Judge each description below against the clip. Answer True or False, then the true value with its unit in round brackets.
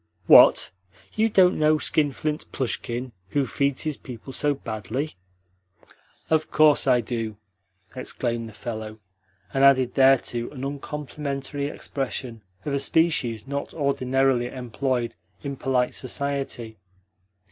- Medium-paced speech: False (115 wpm)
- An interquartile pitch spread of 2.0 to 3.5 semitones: True (2.9 semitones)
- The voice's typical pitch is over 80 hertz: True (135 Hz)